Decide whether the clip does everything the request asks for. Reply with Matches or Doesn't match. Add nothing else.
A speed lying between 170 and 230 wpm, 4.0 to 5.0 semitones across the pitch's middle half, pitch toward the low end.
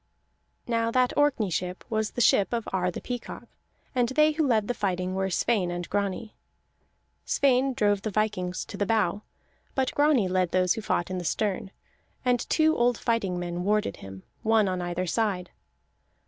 Doesn't match